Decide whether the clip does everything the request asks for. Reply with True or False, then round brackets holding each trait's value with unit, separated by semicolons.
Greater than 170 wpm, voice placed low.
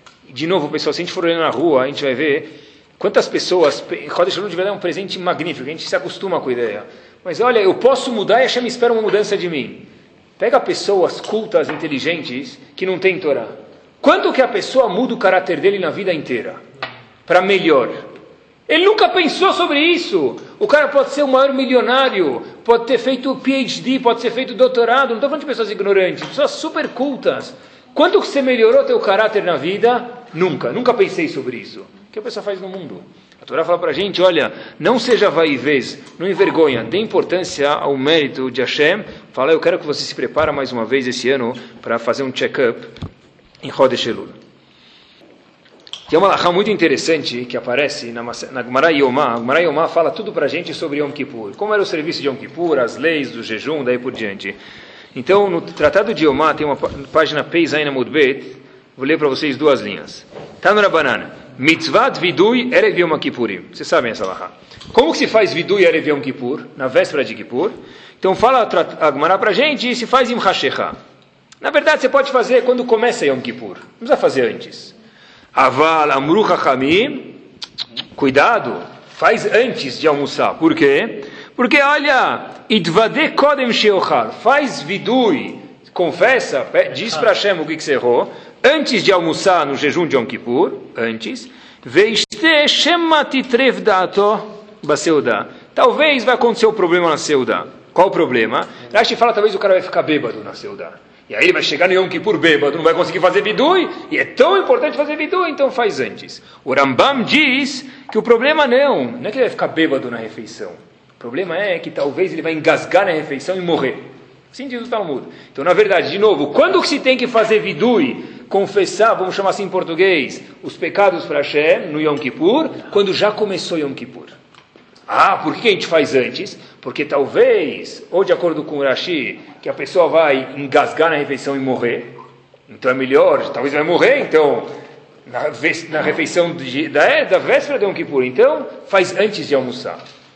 False (185 wpm; 215 Hz)